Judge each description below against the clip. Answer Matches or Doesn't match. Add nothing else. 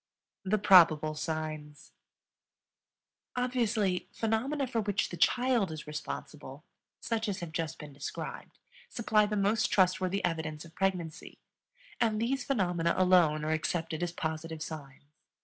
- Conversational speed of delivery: Doesn't match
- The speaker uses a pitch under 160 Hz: Doesn't match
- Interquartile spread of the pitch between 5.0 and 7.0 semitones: Matches